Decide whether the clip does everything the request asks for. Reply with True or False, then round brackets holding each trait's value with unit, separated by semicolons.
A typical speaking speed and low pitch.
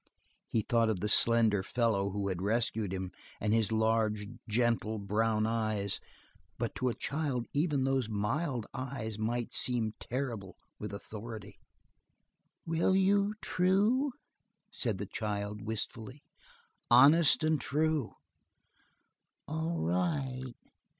False (115 wpm; 115 Hz)